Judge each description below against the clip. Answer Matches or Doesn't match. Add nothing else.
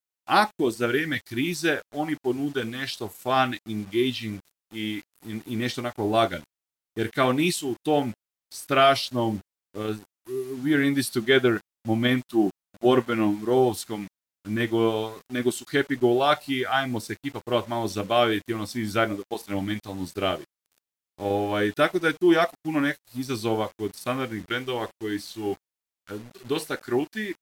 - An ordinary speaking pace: Matches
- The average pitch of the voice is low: Matches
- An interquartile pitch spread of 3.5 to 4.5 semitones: Matches